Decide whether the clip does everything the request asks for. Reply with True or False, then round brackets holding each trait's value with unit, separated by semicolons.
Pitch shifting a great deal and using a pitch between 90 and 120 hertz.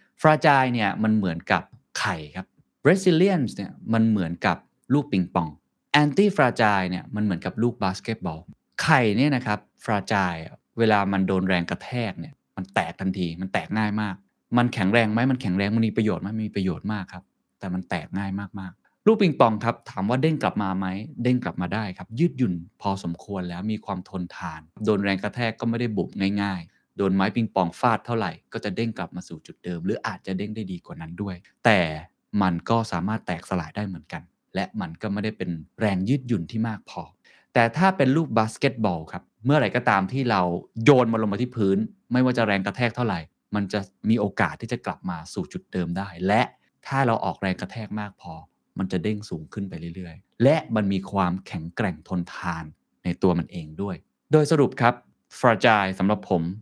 False (3.9 semitones; 100 Hz)